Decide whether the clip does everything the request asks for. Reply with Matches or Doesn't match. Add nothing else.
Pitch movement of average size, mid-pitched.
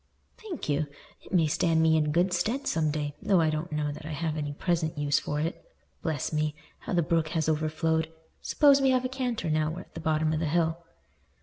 Doesn't match